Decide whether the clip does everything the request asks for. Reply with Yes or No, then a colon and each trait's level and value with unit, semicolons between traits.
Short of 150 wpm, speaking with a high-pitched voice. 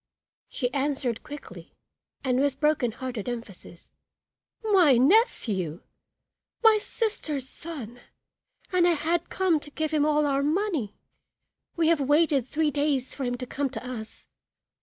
Yes: average, 140 wpm; very high, 285 Hz